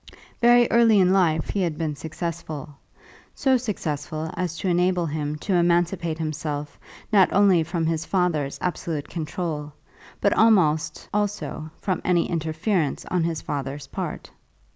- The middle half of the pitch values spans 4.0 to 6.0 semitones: No, average, 3.3 semitones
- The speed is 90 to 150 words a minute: Yes, average, 140 wpm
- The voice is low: No, medium, 170 Hz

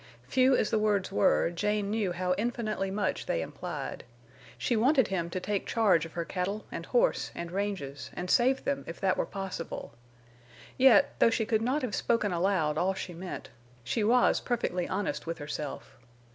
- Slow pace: No, average, 180 wpm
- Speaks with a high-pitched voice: Yes, high, 200 Hz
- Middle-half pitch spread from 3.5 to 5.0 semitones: Yes, average, 4.4 semitones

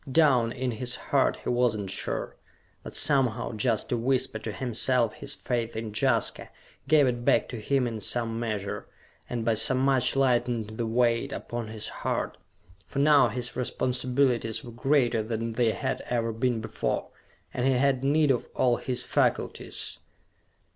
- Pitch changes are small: Yes, narrow, 2.3 semitones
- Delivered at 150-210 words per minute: Yes, average, 165 wpm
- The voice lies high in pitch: No, low, 120 Hz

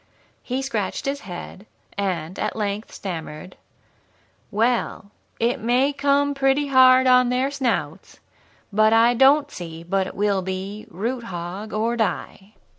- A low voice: No, high, 225 Hz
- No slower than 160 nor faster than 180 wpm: No, slow, 135 wpm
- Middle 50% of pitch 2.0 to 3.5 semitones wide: No, average, 5.1 semitones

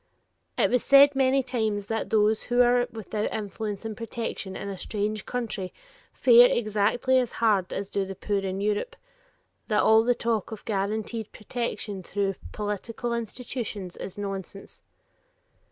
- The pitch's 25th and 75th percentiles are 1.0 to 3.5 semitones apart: Yes, average, 2.8 semitones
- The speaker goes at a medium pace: Yes, average, 150 wpm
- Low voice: No, high, 215 Hz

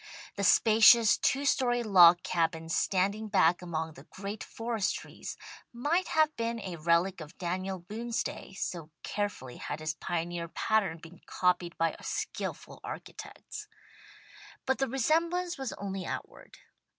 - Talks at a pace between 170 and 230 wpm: No, average, 140 wpm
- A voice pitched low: No, high, 195 Hz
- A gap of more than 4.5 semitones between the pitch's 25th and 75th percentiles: Yes, wide, 5.5 semitones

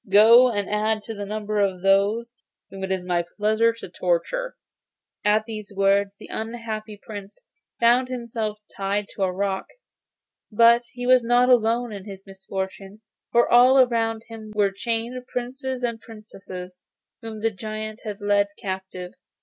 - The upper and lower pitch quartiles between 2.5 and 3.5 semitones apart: Yes, average, 2.9 semitones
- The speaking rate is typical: Yes, average, 155 wpm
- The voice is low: No, high, 215 Hz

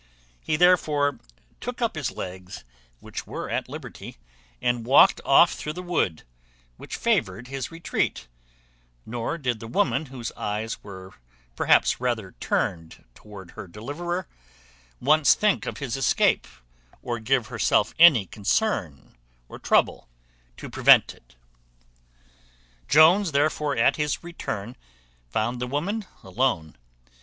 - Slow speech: Yes, slow, 125 wpm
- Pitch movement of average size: No, wide, 6.8 semitones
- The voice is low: Yes, low, 125 Hz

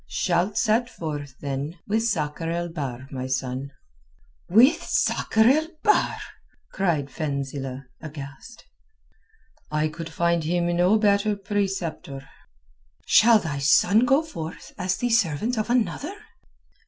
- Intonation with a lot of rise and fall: Yes, wide, 6.9 semitones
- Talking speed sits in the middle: No, slow, 120 wpm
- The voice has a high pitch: No, medium, 170 Hz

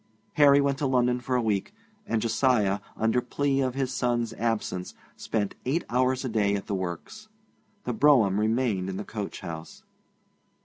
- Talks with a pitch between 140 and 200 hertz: No, low, 120 Hz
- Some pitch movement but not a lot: Yes, average, 4.2 semitones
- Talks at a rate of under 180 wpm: Yes, average, 170 wpm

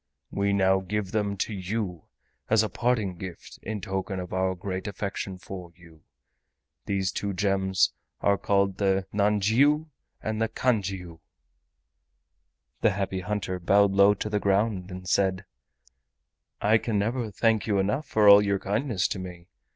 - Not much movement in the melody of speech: Yes, narrow, 2.0 semitones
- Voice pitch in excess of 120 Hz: No, low, 100 Hz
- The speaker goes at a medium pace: Yes, average, 150 wpm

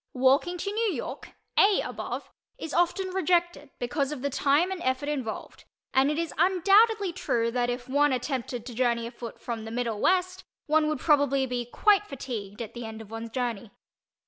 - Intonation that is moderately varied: No, wide, 6.4 semitones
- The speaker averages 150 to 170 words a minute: No, average, 185 wpm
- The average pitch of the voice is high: Yes, very high, 275 Hz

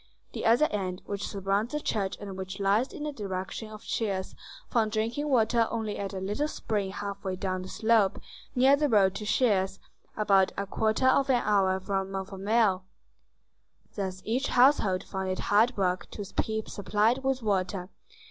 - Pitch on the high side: Yes, high, 205 Hz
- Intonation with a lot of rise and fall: No, average, 3.1 semitones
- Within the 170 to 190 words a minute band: Yes, average, 175 wpm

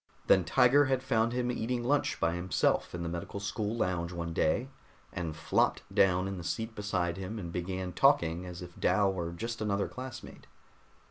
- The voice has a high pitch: No, very low, 95 Hz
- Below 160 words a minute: No, average, 185 wpm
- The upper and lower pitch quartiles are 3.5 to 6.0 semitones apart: Yes, average, 4.9 semitones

